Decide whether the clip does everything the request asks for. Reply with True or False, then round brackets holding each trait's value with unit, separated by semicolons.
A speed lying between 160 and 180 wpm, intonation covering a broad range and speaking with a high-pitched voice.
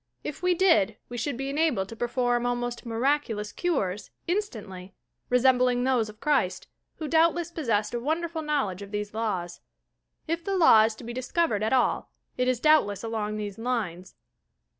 True (170 wpm; 6.0 semitones; 245 Hz)